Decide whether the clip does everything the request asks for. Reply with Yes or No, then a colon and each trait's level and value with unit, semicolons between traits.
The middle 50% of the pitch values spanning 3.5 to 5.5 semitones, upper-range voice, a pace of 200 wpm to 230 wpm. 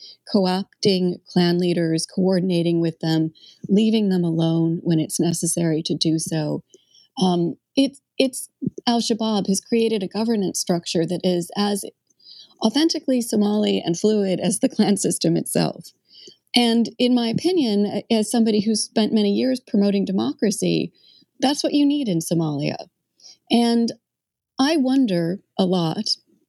No: average, 5.0 semitones; high, 205 Hz; slow, 135 wpm